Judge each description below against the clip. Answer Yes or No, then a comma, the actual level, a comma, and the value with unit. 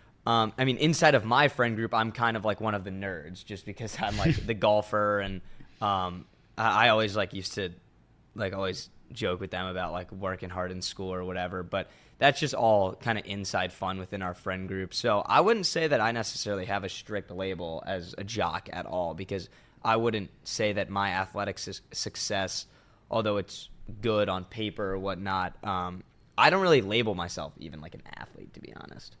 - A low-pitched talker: Yes, low, 100 Hz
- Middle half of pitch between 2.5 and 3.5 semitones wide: Yes, average, 3.0 semitones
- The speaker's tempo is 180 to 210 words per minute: Yes, fast, 205 wpm